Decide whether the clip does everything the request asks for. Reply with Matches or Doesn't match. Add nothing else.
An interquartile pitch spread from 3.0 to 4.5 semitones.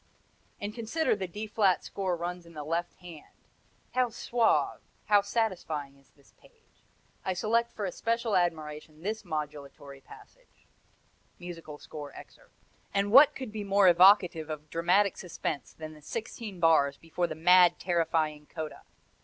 Doesn't match